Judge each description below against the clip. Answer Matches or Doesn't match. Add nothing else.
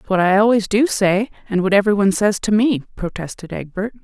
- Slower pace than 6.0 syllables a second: Doesn't match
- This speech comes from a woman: Matches